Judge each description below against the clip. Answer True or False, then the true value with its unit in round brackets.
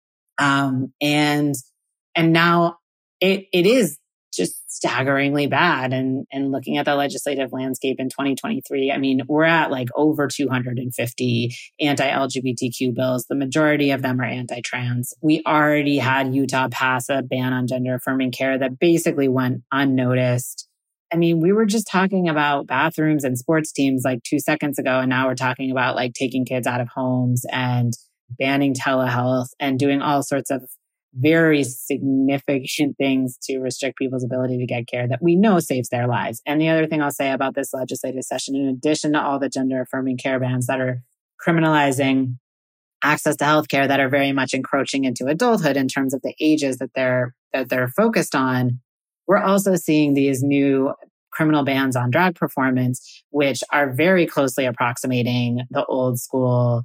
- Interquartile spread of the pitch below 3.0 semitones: True (2.4 semitones)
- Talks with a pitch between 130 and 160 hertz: True (135 Hz)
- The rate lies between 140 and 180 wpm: True (170 wpm)